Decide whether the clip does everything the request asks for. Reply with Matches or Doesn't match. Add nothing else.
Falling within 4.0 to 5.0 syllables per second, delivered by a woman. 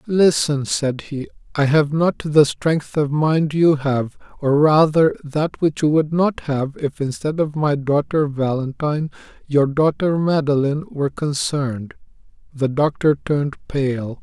Doesn't match